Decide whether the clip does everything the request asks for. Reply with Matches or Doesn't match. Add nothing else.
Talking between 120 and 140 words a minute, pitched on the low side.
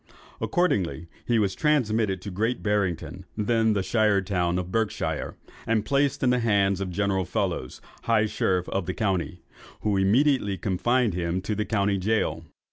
Doesn't match